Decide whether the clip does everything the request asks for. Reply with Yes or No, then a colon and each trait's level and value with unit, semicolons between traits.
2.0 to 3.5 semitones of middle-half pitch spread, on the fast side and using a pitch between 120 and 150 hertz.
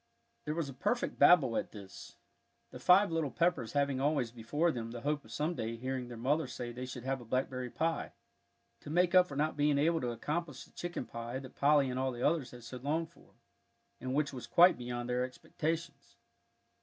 No: average, 4.3 semitones; fast, 210 wpm; low, 135 Hz